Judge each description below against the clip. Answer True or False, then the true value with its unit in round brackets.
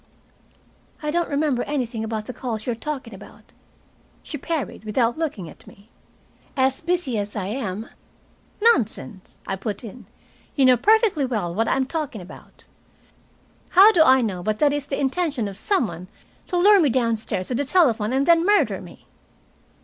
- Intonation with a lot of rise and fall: True (5.8 semitones)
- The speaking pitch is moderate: False (255 Hz)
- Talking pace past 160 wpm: True (180 wpm)